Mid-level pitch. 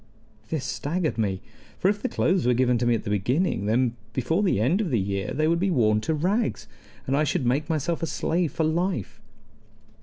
Yes: medium, 145 Hz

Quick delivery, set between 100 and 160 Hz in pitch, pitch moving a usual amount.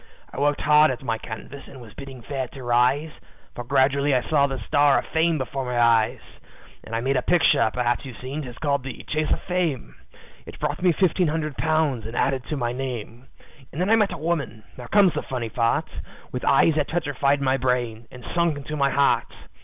Yes: fast, 210 wpm; low, 135 Hz; average, 3.6 semitones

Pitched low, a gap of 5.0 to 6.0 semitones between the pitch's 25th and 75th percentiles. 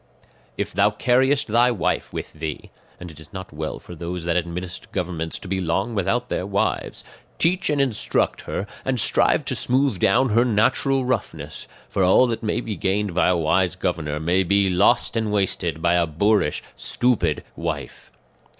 Yes: very low, 95 Hz; average, 5.3 semitones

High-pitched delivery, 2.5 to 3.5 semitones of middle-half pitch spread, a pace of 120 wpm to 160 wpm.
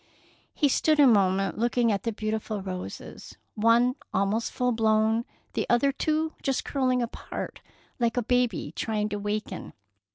Yes: high, 230 Hz; average, 2.9 semitones; average, 150 wpm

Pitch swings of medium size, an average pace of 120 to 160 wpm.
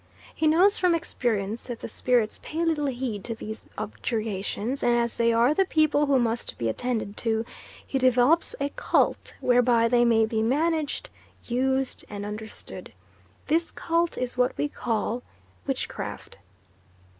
Yes: average, 4.5 semitones; average, 150 wpm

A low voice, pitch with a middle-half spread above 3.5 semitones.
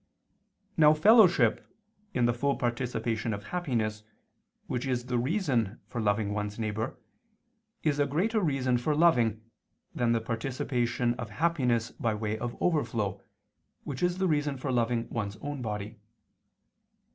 Yes: low, 120 Hz; average, 4.6 semitones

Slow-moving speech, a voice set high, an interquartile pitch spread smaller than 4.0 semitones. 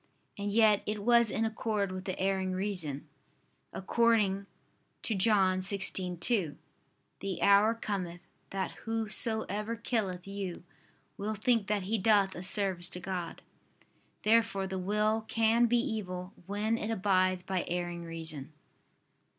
Yes: slow, 130 wpm; high, 200 Hz; average, 2.9 semitones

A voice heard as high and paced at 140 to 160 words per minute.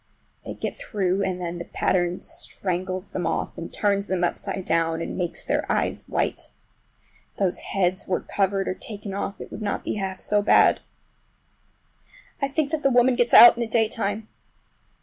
No: high, 195 Hz; average, 175 wpm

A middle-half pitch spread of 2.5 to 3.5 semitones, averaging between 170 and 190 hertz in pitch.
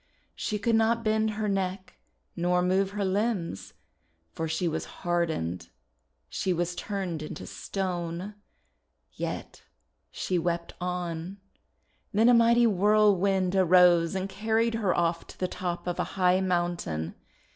Yes: average, 3.0 semitones; medium, 185 Hz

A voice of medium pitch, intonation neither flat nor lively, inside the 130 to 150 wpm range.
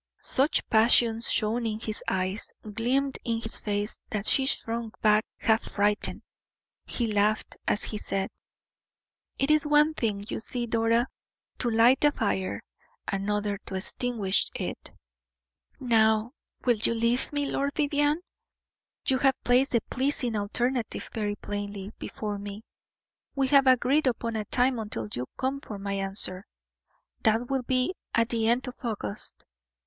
No: high, 230 Hz; average, 3.7 semitones; average, 145 wpm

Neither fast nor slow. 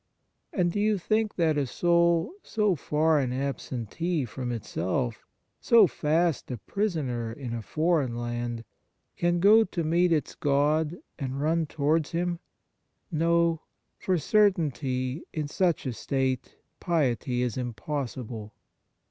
No: slow, 130 wpm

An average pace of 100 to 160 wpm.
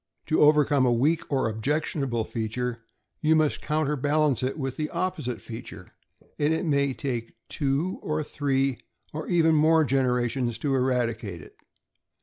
Yes: average, 145 wpm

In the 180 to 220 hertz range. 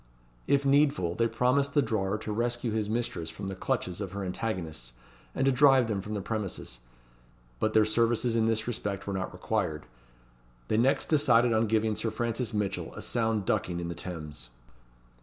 No: low, 110 Hz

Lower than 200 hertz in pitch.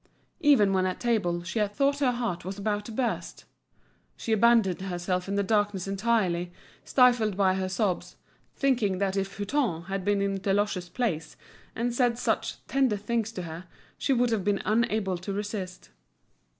No: high, 205 Hz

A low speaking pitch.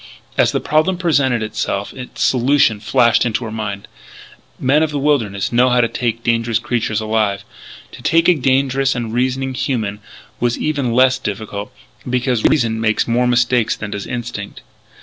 Yes: low, 120 Hz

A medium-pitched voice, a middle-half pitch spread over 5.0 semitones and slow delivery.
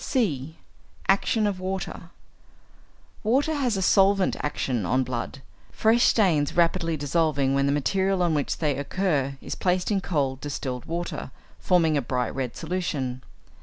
No: medium, 165 Hz; wide, 5.6 semitones; average, 145 wpm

